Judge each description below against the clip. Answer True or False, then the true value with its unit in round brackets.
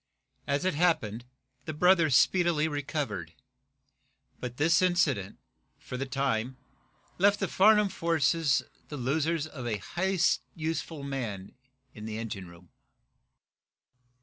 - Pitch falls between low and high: True (145 Hz)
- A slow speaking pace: True (120 wpm)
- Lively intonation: True (5.9 semitones)